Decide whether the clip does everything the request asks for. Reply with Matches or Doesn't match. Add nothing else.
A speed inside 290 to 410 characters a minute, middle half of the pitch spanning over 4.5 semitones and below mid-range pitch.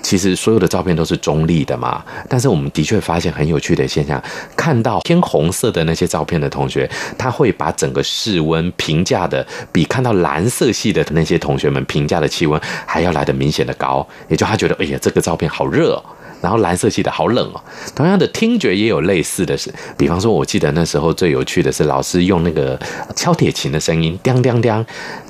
Matches